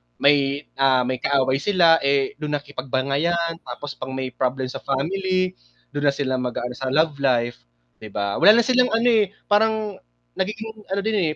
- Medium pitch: Yes, medium, 145 Hz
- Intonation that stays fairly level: No, wide, 6.3 semitones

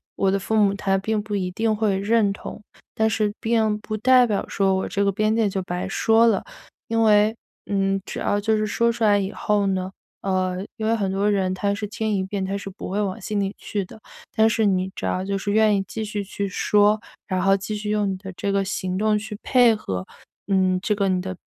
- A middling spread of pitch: No, narrow, 2.0 semitones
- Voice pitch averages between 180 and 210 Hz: Yes, high, 205 Hz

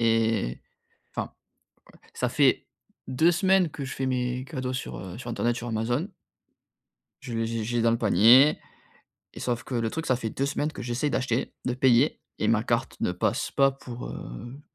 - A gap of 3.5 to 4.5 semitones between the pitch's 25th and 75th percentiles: No, average, 2.8 semitones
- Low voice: Yes, low, 125 Hz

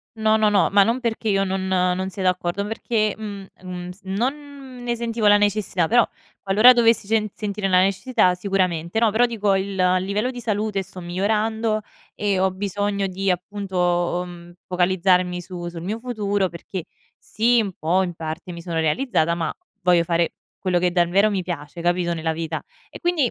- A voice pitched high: Yes, high, 195 Hz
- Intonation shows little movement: No, average, 3.3 semitones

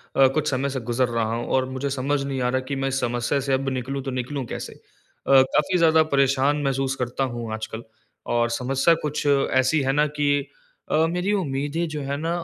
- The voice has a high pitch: No, low, 135 Hz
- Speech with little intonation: Yes, narrow, 2.1 semitones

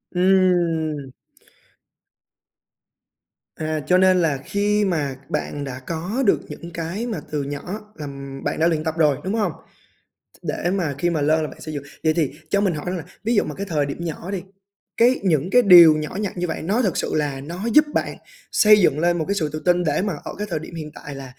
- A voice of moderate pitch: Yes, medium, 170 Hz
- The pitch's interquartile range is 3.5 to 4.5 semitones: Yes, average, 4.0 semitones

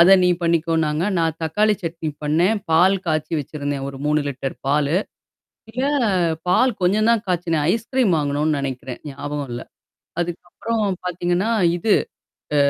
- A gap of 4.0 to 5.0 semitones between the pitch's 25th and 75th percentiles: Yes, average, 4.3 semitones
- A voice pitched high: No, medium, 165 Hz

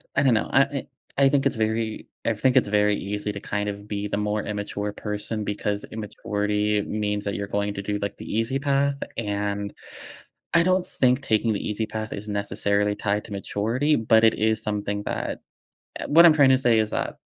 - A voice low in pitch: Yes, low, 105 Hz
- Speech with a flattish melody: Yes, narrow, 2.0 semitones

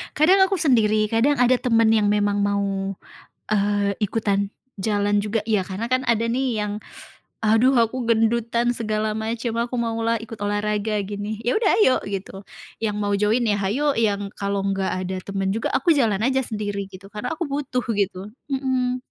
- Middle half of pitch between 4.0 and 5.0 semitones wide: No, average, 2.8 semitones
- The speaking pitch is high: Yes, high, 215 Hz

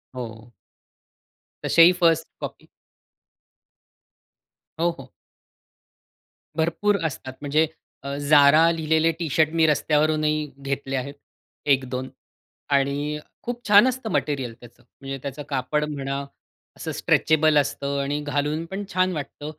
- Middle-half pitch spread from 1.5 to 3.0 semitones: Yes, narrow, 2.6 semitones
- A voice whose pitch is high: No, medium, 150 Hz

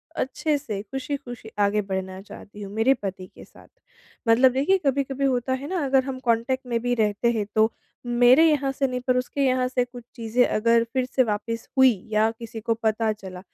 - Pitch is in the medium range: No, high, 245 Hz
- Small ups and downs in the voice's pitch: No, average, 3.2 semitones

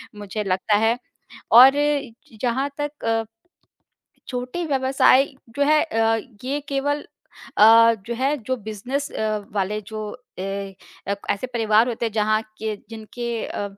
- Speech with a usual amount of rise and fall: Yes, average, 4.0 semitones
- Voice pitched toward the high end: Yes, high, 230 Hz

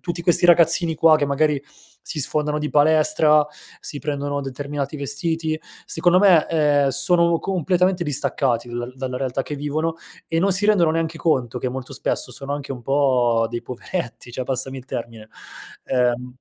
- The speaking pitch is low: No, medium, 145 Hz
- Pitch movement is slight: No, average, 3.9 semitones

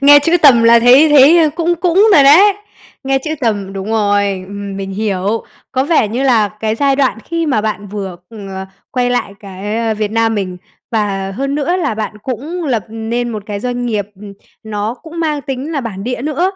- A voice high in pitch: Yes, high, 230 Hz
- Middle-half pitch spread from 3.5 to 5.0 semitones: No, wide, 5.4 semitones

